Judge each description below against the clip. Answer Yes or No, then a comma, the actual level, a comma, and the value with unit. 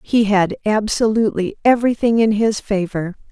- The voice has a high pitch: Yes, high, 210 Hz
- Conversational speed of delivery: No, slow, 125 wpm